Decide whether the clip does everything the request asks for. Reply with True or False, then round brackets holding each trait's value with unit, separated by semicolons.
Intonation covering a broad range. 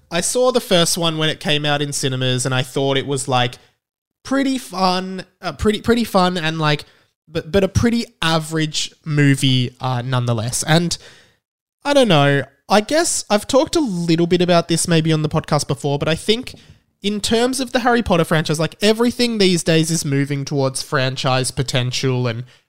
True (6.0 semitones)